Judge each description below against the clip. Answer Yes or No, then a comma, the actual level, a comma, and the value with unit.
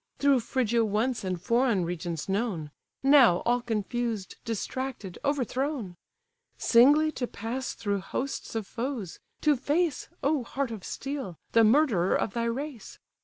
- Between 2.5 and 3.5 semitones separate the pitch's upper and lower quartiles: No, average, 4.8 semitones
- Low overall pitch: No, high, 235 Hz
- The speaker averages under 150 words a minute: Yes, slow, 135 wpm